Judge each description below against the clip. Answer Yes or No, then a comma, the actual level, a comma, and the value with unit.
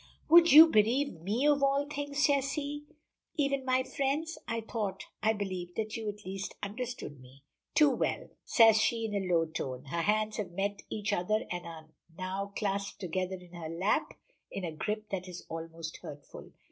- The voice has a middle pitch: No, high, 210 Hz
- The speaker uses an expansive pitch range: Yes, wide, 6.5 semitones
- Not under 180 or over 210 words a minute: Yes, average, 185 wpm